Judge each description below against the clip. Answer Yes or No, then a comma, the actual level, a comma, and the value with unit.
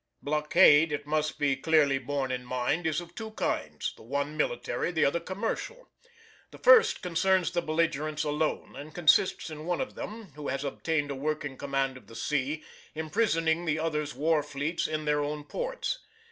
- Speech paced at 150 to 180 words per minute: Yes, average, 175 wpm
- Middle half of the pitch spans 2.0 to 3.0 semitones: Yes, average, 2.7 semitones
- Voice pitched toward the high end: No, medium, 155 Hz